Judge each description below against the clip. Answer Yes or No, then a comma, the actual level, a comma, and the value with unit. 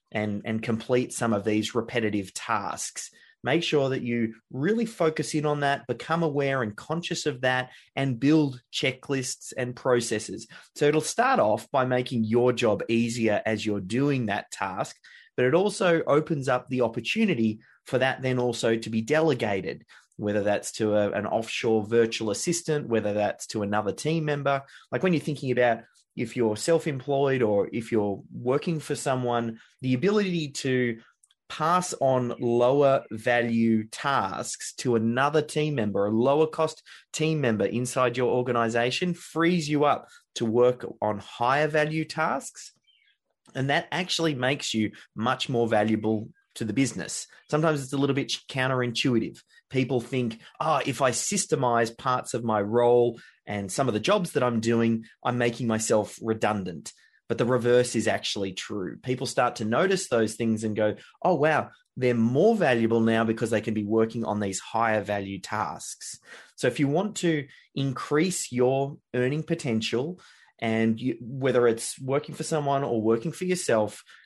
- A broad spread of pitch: No, average, 4.5 semitones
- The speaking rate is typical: Yes, average, 165 wpm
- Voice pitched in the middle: No, low, 125 Hz